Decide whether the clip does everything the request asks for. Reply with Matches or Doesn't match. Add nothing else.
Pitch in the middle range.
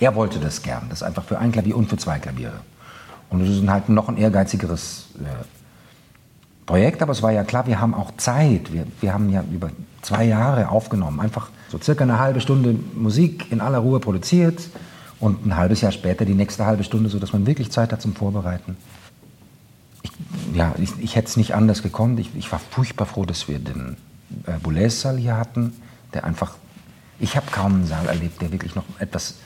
Doesn't match